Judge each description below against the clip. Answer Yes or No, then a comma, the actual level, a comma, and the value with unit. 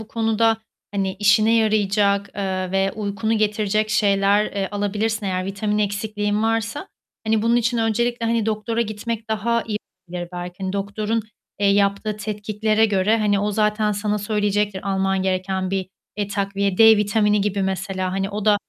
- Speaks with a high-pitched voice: Yes, high, 210 Hz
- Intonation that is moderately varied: No, narrow, 1.7 semitones